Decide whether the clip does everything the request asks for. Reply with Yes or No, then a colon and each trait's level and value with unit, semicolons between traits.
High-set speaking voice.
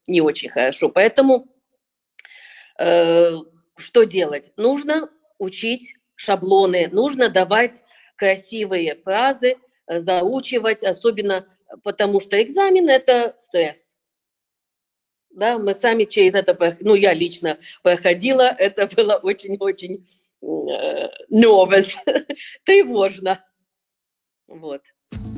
Yes: high, 200 Hz